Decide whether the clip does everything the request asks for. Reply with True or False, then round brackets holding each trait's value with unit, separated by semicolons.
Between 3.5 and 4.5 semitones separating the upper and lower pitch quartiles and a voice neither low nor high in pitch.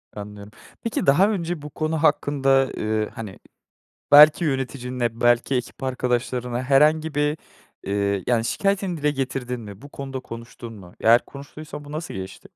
False (4.2 semitones; 130 Hz)